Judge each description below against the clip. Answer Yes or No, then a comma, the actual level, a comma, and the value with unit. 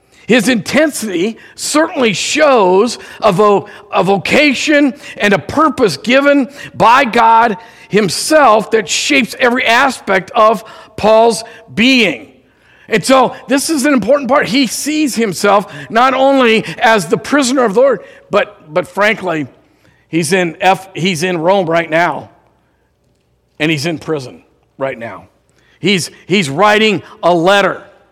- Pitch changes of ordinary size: No, wide, 5.8 semitones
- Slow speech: Yes, slow, 130 wpm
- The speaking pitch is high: Yes, high, 220 Hz